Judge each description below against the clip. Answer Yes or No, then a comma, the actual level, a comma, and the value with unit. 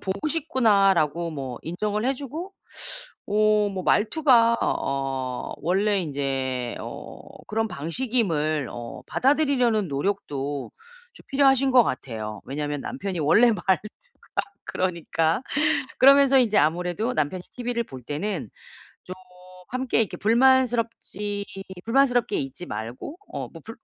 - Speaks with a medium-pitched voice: No, high, 205 Hz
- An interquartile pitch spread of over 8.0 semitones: Yes, wide, 8.6 semitones